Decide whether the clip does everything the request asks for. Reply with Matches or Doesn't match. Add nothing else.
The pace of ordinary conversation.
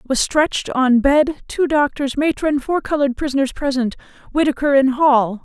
Matches